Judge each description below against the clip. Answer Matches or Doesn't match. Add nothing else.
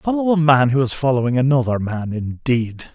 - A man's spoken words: Matches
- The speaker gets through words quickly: Doesn't match